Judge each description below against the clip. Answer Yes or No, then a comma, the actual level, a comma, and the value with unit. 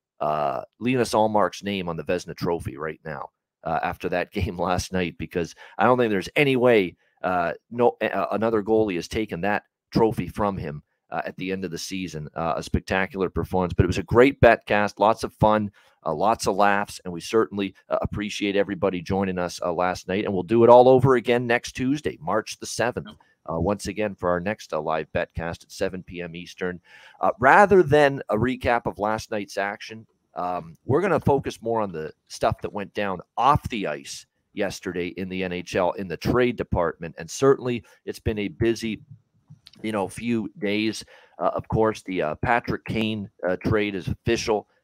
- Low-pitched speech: Yes, low, 105 Hz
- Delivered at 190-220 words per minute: Yes, average, 200 wpm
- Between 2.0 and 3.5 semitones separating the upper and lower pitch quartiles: No, average, 4.0 semitones